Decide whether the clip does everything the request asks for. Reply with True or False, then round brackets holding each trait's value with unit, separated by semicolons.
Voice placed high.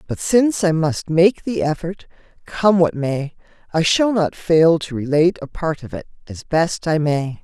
False (165 Hz)